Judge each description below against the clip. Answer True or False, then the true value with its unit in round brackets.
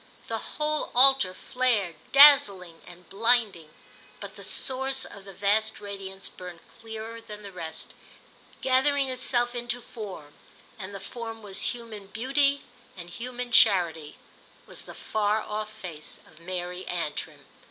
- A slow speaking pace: True (130 wpm)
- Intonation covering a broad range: False (5.0 semitones)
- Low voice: False (215 Hz)